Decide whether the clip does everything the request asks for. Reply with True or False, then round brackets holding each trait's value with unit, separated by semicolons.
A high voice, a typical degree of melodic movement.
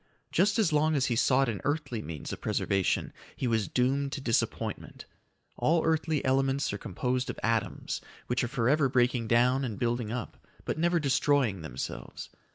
False (130 Hz; 3.8 semitones)